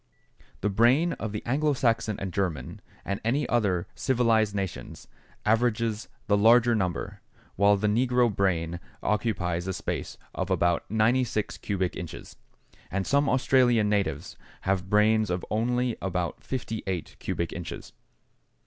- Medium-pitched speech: No, low, 105 Hz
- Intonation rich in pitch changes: No, average, 4.0 semitones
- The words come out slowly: Yes, slow, 130 wpm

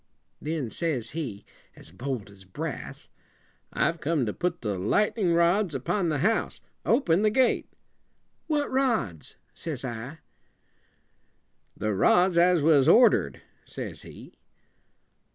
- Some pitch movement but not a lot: No, wide, 7.6 semitones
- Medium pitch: Yes, medium, 160 Hz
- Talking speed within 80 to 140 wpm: Yes, slow, 135 wpm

